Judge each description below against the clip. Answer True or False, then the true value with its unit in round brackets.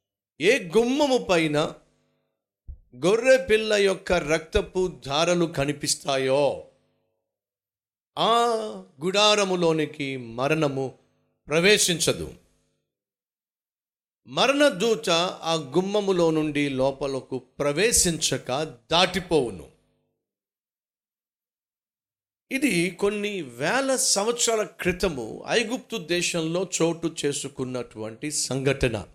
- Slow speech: True (60 wpm)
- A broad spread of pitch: True (6.8 semitones)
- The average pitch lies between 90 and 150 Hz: False (165 Hz)